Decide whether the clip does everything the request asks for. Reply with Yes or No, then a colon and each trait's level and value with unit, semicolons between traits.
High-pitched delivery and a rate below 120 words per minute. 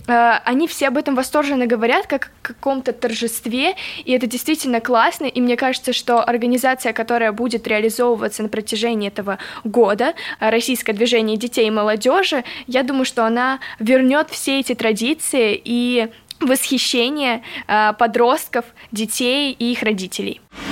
No: high, 245 Hz; average, 135 wpm